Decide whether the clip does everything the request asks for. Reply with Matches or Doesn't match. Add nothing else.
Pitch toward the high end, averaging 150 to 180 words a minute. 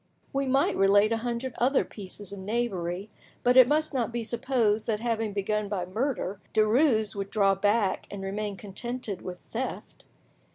Matches